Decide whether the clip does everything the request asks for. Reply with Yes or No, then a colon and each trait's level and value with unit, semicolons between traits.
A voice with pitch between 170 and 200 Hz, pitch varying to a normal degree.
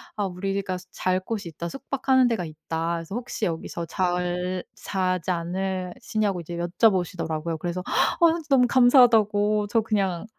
Yes: medium, 185 Hz; average, 3.7 semitones